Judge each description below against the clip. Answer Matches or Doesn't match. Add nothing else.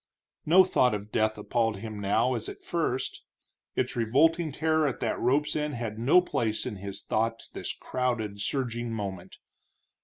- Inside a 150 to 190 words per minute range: Matches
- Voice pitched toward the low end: Matches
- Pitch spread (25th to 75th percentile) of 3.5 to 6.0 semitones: Matches